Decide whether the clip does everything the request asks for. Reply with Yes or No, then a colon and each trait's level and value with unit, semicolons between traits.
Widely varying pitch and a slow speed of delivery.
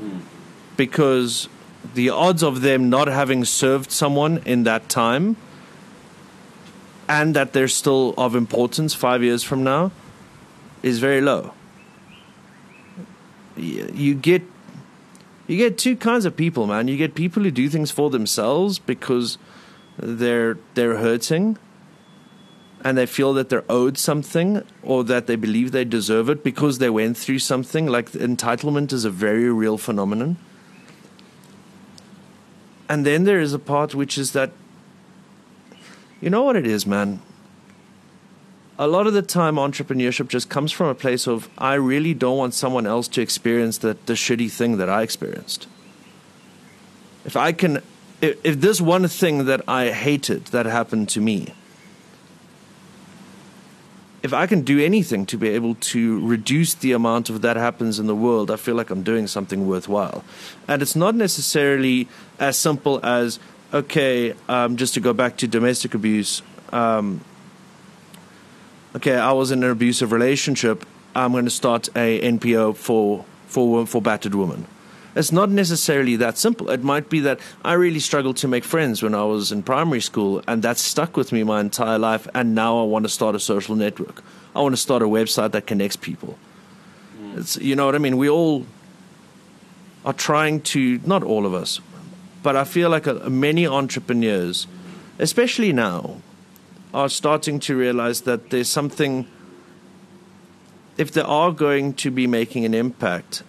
No: wide, 6.0 semitones; average, 160 wpm